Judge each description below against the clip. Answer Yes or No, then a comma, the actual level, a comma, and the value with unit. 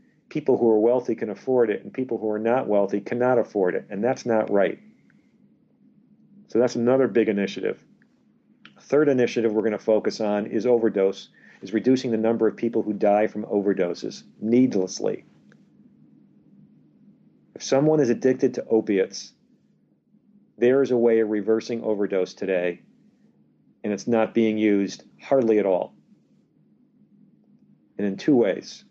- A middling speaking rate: Yes, average, 145 wpm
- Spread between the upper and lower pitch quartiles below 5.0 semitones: Yes, average, 3.9 semitones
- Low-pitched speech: Yes, low, 115 Hz